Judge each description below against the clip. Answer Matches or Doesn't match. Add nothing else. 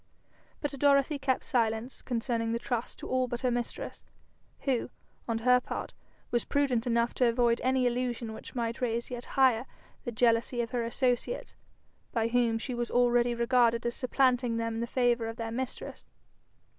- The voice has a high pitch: Matches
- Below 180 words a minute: Matches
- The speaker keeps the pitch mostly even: Matches